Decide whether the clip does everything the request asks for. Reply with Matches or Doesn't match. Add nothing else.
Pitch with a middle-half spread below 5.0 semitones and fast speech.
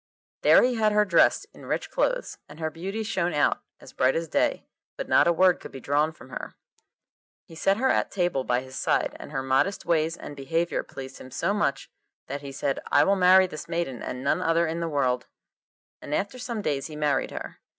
Doesn't match